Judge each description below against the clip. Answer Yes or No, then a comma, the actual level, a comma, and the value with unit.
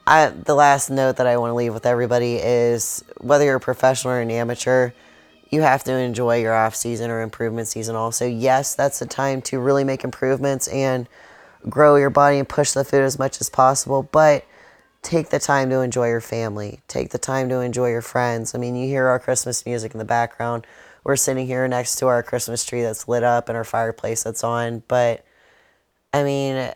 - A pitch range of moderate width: No, narrow, 2.3 semitones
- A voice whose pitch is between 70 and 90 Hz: No, low, 125 Hz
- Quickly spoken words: Yes, fast, 210 wpm